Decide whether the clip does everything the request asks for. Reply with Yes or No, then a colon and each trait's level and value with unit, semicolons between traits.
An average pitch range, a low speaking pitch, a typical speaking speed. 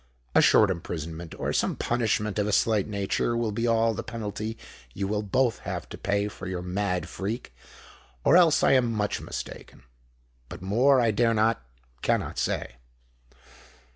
Yes: average, 4.1 semitones; low, 105 Hz; average, 150 wpm